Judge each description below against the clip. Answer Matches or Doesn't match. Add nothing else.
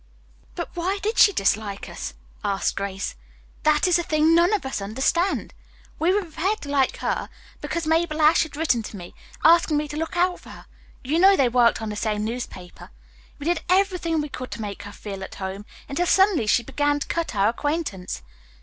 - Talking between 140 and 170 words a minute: Doesn't match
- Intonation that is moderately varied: Doesn't match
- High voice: Matches